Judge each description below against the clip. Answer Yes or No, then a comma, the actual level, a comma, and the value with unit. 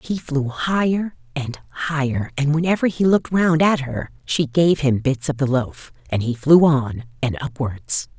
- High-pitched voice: No, medium, 145 Hz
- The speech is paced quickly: No, average, 185 wpm